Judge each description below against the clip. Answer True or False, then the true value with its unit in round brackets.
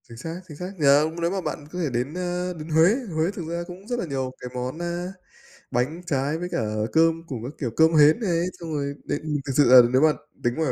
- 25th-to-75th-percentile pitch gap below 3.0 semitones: False (3.6 semitones)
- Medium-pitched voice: True (160 Hz)